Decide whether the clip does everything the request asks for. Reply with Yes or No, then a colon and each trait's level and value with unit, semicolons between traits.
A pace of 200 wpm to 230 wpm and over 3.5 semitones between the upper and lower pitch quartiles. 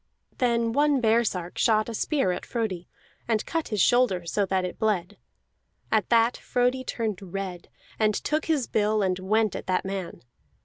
No: average, 170 wpm; average, 4.0 semitones